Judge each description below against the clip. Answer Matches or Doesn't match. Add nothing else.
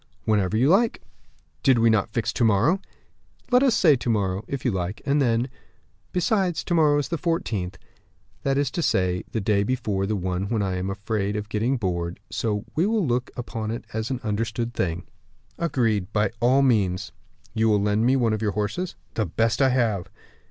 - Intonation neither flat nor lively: Matches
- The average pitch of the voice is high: Doesn't match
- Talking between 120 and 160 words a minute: Doesn't match